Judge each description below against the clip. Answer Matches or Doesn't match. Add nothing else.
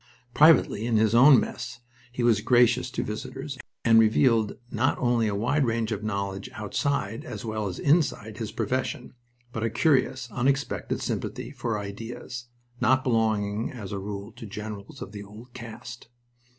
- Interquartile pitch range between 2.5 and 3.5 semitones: Matches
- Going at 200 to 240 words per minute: Doesn't match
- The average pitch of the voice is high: Doesn't match